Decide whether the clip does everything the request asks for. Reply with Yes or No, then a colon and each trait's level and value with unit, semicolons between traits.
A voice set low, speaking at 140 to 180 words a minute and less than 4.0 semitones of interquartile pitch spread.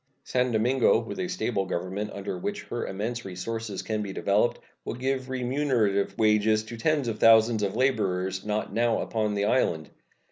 Yes: low, 110 Hz; average, 170 wpm; average, 3.6 semitones